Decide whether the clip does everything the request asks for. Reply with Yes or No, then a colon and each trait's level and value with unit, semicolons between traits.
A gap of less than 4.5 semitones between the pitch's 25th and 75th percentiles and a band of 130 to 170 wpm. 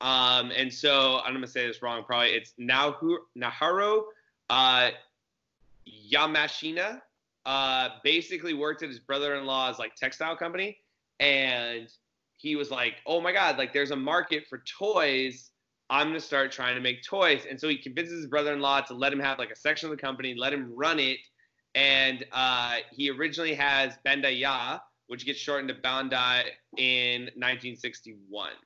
Yes: average, 3.1 semitones; average, 160 wpm